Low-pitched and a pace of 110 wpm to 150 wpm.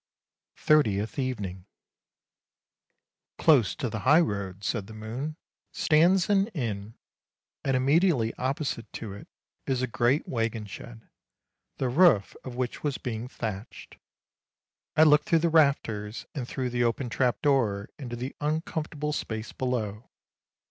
Yes: low, 125 Hz; average, 140 wpm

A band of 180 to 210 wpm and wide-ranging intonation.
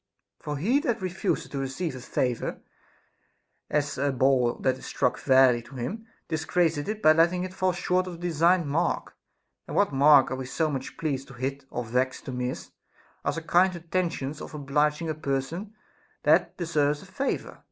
No: average, 185 wpm; average, 4.8 semitones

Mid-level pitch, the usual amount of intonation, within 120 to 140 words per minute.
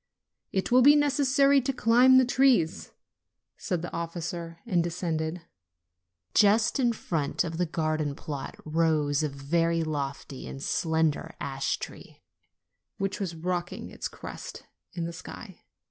No: medium, 170 Hz; wide, 5.8 semitones; slow, 135 wpm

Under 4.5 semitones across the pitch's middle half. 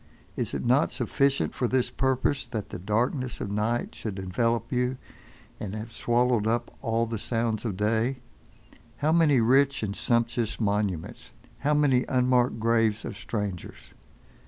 Yes: average, 2.9 semitones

